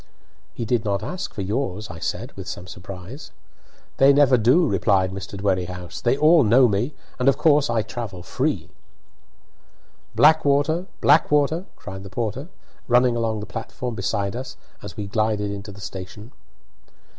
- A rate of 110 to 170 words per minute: Yes, average, 155 wpm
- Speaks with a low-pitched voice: Yes, low, 115 Hz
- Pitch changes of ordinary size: No, wide, 5.7 semitones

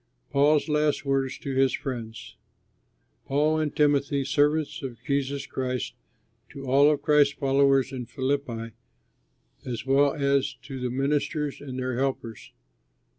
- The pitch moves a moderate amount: No, narrow, 1.8 semitones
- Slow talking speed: Yes, slow, 130 wpm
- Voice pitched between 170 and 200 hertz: No, medium, 140 Hz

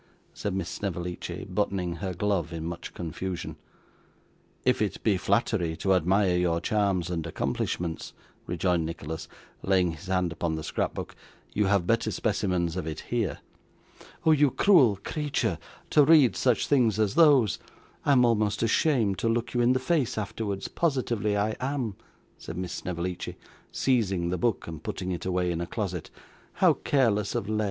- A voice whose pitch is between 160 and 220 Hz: No, low, 100 Hz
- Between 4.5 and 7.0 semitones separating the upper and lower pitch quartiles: Yes, average, 4.8 semitones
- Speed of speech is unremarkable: Yes, average, 160 wpm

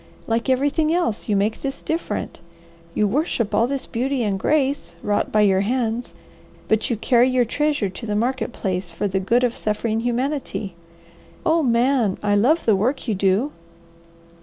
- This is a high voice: Yes, high, 235 Hz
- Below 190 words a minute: Yes, average, 170 wpm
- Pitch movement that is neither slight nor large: Yes, average, 4.4 semitones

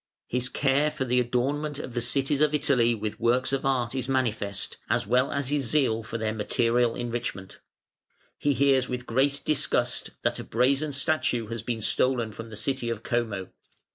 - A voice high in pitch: No, low, 125 Hz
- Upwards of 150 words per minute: Yes, average, 180 wpm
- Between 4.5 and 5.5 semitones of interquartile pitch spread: No, average, 2.9 semitones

